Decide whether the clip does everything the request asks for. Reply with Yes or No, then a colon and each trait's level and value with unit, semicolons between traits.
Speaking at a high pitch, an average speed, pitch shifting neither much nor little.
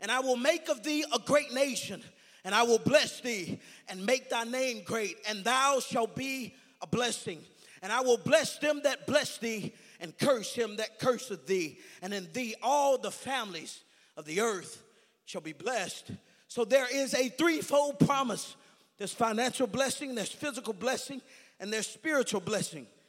Yes: high, 245 Hz; average, 175 wpm; average, 4.2 semitones